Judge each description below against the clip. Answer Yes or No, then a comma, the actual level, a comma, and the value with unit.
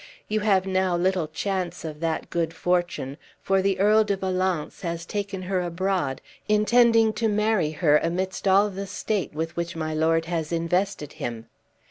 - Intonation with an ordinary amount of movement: Yes, average, 3.2 semitones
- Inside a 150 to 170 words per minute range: Yes, average, 160 wpm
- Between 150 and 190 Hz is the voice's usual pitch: Yes, medium, 185 Hz